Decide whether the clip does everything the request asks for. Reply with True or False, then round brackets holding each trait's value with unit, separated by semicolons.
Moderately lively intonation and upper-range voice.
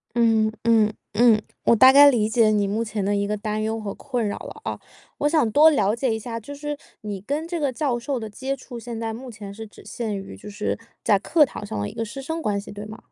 True (3.9 semitones; 225 Hz)